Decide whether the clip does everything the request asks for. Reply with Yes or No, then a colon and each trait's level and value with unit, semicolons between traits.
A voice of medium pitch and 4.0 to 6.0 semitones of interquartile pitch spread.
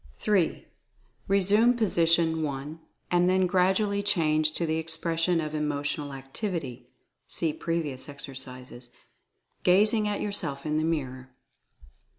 Yes: medium, 160 Hz; average, 4.4 semitones